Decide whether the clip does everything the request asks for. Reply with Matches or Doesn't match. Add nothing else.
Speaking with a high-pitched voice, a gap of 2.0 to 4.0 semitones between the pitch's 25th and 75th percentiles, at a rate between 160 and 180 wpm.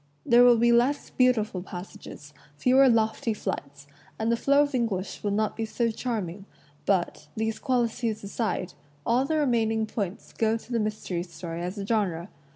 Matches